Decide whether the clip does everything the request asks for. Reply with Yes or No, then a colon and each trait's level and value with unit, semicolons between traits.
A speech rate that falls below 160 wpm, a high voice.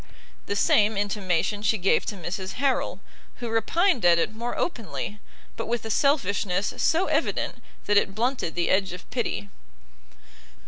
Yes: average, 150 wpm; high, 205 Hz